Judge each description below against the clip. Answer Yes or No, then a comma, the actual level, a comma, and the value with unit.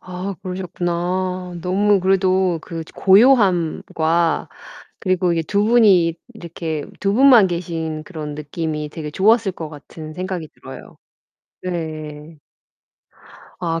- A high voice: No, medium, 175 Hz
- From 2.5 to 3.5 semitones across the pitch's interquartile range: Yes, average, 2.8 semitones